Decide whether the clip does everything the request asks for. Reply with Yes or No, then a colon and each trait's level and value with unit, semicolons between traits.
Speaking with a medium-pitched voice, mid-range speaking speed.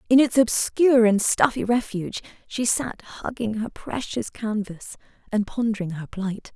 No: high, 220 Hz; average, 145 wpm